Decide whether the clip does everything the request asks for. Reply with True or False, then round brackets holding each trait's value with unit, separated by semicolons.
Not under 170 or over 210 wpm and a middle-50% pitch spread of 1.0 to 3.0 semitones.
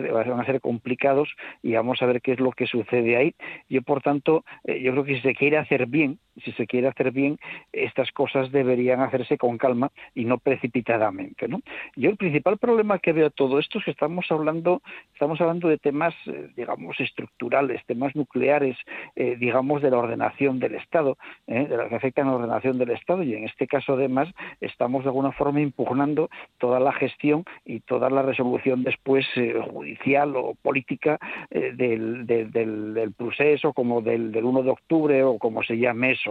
True (190 wpm; 2.7 semitones)